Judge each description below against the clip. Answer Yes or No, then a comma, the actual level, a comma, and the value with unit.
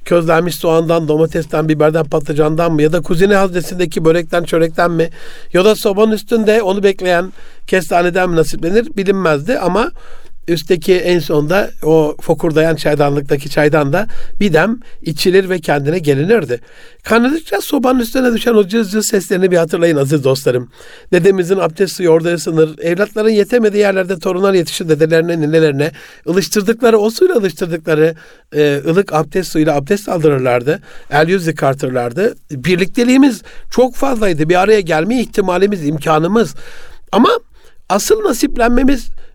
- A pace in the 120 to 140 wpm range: Yes, average, 130 wpm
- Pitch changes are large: No, average, 4.7 semitones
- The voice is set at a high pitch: No, medium, 180 Hz